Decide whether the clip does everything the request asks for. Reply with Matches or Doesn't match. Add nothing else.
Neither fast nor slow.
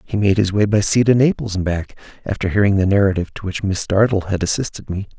Doesn't match